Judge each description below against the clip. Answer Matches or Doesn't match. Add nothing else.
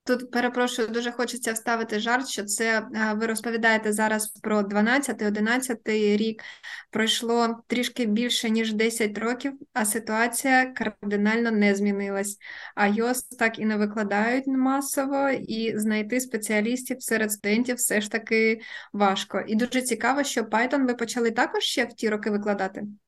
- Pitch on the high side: Matches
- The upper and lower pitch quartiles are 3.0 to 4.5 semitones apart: Doesn't match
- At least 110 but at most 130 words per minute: Doesn't match